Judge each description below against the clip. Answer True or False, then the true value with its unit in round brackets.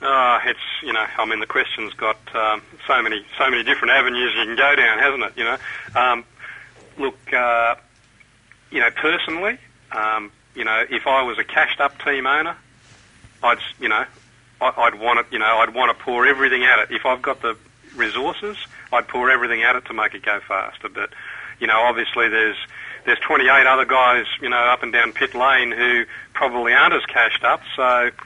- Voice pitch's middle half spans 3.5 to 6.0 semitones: False (2.8 semitones)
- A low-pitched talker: True (120 Hz)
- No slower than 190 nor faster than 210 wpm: True (200 wpm)